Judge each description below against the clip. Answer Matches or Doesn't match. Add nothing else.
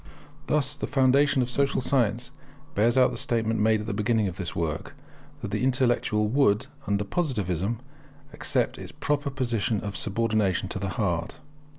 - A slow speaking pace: Doesn't match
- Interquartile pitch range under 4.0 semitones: Doesn't match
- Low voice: Matches